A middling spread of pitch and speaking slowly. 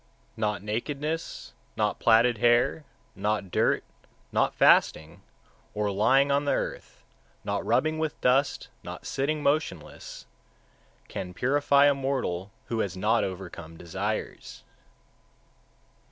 No: wide, 6.3 semitones; slow, 115 wpm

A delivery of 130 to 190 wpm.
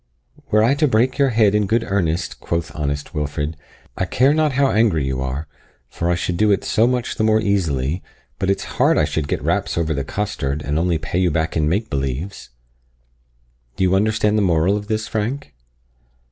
No: average, 200 wpm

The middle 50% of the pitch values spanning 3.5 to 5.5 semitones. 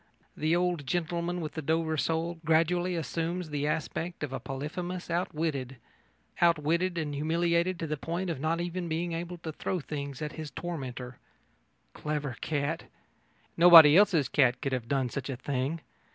No: average, 3.1 semitones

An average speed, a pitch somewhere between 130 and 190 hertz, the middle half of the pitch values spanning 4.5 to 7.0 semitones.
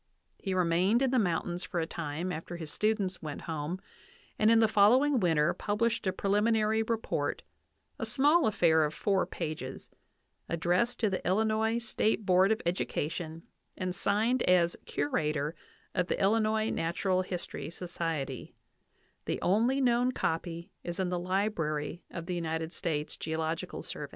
Yes: average, 155 wpm; medium, 185 Hz; average, 4.8 semitones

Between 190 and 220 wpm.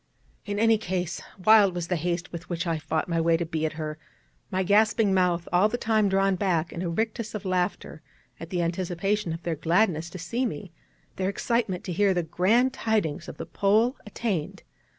Yes: average, 200 wpm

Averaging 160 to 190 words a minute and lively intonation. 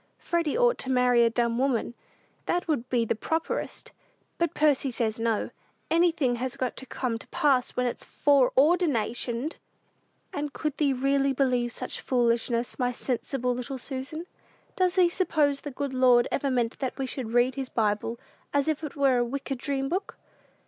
No: average, 170 wpm; average, 3.2 semitones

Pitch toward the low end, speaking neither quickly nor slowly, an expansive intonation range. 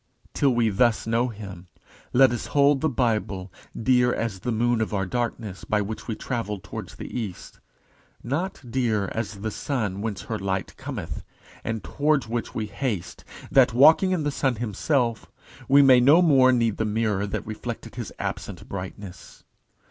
No: low, 115 Hz; average, 170 wpm; average, 3.6 semitones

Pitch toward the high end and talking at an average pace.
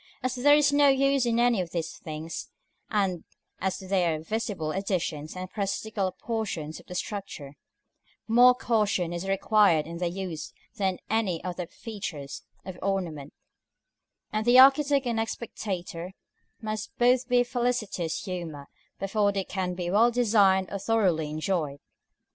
Yes: high, 195 Hz; average, 150 wpm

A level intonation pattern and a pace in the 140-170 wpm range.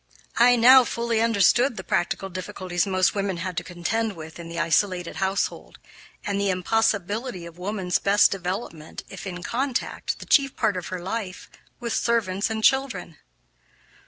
No: average, 4.2 semitones; average, 160 wpm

